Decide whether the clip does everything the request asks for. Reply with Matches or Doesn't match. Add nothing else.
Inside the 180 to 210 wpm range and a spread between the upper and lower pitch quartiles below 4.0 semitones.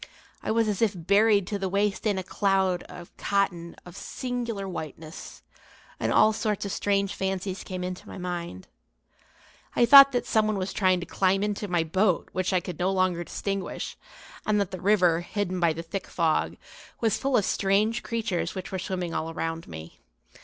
Matches